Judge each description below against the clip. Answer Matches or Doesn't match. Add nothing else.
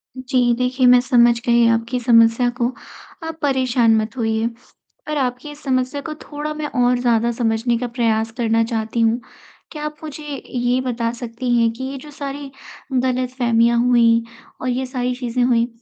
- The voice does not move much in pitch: Matches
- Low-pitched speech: Doesn't match